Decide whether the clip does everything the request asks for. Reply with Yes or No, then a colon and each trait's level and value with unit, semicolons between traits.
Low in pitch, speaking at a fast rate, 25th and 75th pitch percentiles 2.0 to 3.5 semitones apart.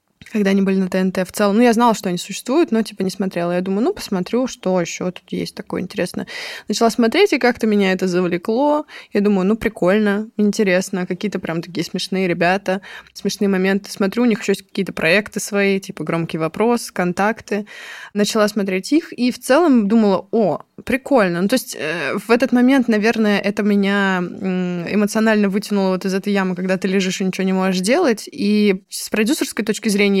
No: high, 200 Hz; fast, 190 wpm; average, 3.2 semitones